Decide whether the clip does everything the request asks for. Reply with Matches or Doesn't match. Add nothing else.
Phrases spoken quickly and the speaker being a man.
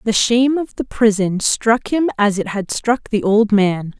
Doesn't match